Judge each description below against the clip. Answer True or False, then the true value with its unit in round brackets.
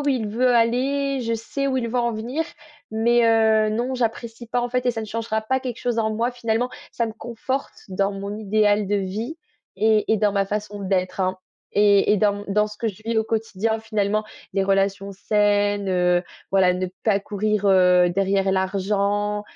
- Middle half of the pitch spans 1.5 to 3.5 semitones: True (2.6 semitones)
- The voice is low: False (215 Hz)